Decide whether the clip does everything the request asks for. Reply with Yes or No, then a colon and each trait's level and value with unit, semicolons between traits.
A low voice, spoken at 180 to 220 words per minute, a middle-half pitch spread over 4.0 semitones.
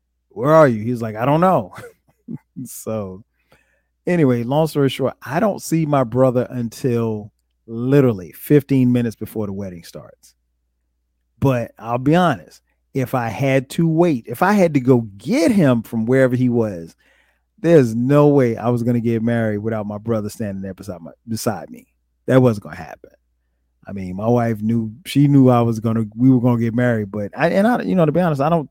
Yes: low, 120 Hz; fast, 205 wpm; average, 4.8 semitones